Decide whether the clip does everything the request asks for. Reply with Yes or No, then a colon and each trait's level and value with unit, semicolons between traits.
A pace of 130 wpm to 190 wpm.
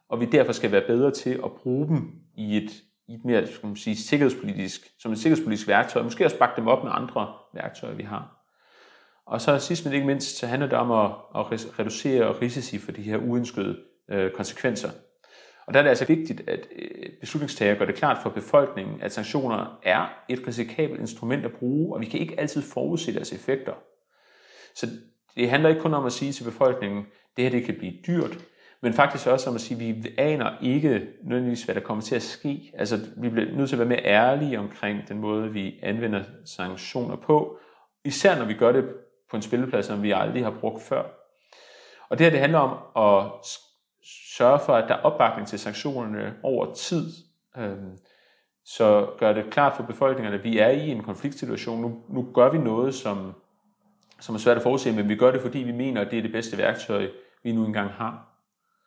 No: average, 205 wpm